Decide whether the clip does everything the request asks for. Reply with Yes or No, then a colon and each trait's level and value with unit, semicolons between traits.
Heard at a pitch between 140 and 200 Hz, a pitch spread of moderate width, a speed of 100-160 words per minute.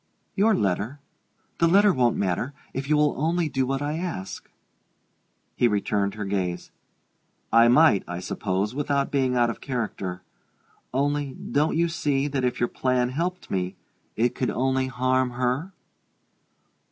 No: low, 130 Hz; average, 4.7 semitones; average, 150 wpm